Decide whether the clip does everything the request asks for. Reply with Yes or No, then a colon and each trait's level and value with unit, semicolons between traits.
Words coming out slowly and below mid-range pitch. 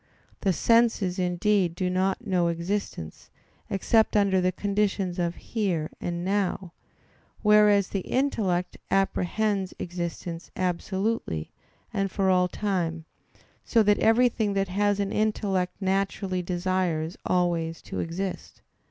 No: slow, 115 wpm; high, 190 Hz